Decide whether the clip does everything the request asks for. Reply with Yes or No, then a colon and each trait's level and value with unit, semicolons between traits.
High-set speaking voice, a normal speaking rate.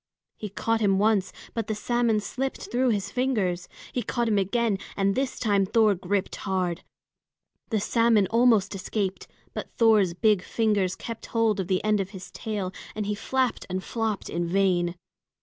Yes: high, 210 Hz; average, 170 wpm